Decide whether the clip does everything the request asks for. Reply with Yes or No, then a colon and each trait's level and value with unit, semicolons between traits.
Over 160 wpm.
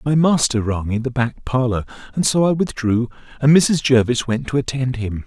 Yes: fast, 205 wpm